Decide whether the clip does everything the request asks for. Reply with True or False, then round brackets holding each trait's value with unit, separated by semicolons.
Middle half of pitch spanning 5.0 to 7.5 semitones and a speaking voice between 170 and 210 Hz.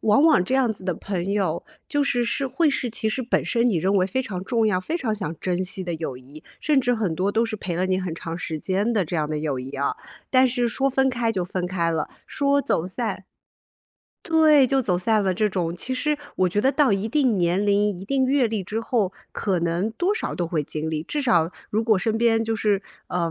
True (5.5 semitones; 205 Hz)